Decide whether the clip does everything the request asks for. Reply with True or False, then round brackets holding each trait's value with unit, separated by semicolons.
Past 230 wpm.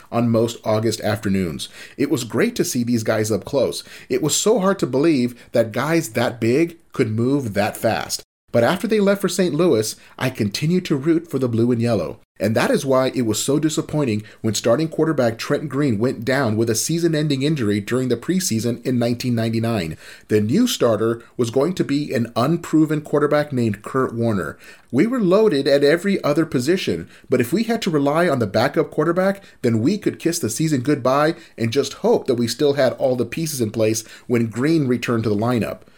False (205 wpm)